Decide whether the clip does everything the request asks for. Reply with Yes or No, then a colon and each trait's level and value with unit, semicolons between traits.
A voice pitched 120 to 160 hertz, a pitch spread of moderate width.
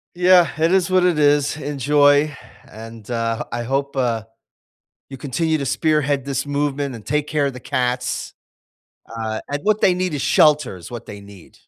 Yes: medium, 140 Hz; average, 3.8 semitones